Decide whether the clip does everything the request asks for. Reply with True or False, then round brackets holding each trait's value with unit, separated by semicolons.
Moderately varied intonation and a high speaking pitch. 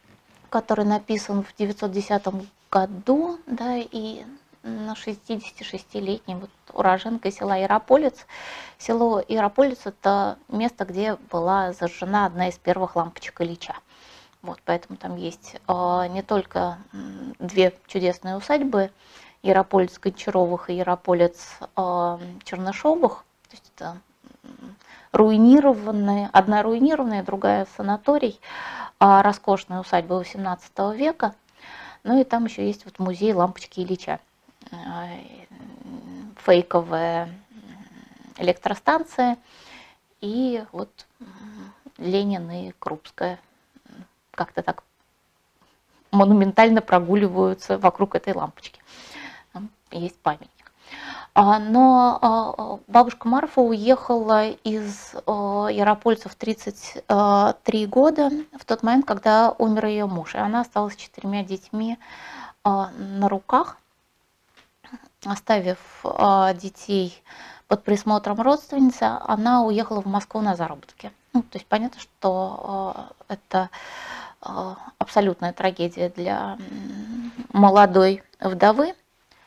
True (3.7 semitones; 205 Hz)